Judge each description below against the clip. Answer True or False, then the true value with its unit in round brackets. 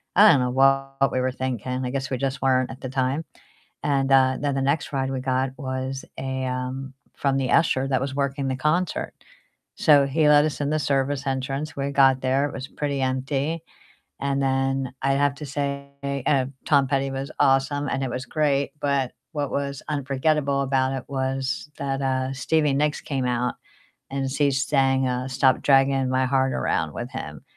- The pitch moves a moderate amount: False (1.1 semitones)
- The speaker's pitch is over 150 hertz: False (135 Hz)